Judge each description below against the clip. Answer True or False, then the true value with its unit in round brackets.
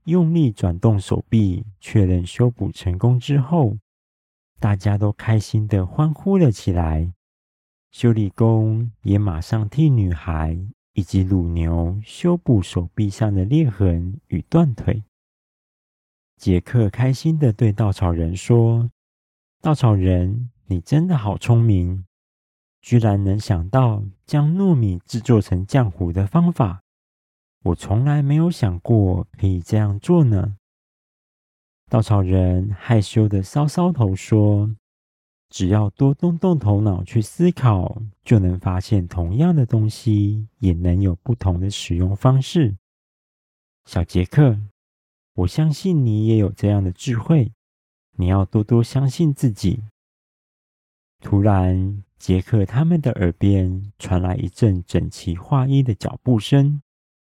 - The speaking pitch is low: True (105 Hz)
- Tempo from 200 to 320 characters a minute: False (190 characters per minute)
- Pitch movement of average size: True (5.0 semitones)